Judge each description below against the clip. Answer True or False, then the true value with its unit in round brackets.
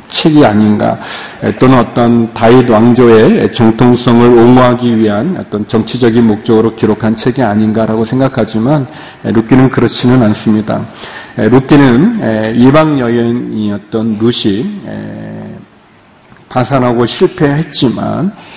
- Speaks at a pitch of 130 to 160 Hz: False (120 Hz)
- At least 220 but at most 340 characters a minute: True (260 characters per minute)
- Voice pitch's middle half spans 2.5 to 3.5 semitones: True (2.9 semitones)